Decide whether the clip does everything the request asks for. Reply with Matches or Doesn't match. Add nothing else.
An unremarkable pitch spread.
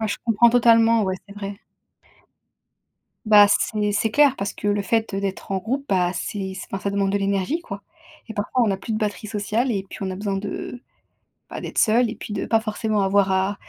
Doesn't match